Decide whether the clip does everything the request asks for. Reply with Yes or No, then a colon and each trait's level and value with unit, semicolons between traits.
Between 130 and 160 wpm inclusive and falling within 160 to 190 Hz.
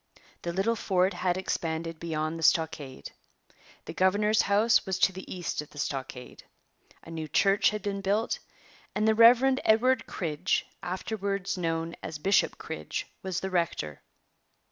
Yes: average, 150 wpm; medium, 185 Hz